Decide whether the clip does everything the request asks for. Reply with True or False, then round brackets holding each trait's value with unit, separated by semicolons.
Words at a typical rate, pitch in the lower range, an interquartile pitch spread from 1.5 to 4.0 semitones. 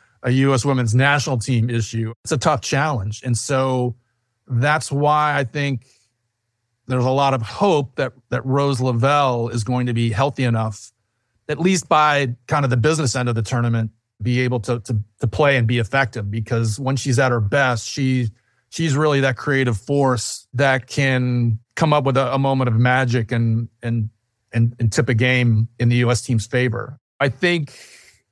True (185 wpm; 125 Hz; 2.7 semitones)